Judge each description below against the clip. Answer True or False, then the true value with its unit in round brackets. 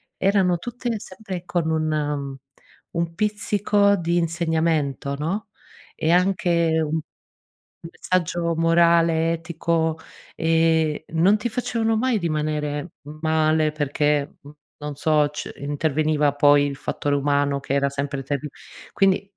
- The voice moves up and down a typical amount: True (3.0 semitones)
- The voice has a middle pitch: True (160 Hz)